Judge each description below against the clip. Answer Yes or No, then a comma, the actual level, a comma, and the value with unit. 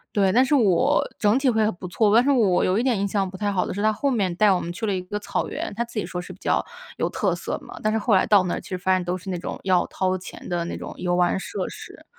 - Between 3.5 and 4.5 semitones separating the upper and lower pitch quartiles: No, average, 3.0 semitones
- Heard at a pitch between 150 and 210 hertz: Yes, high, 195 Hz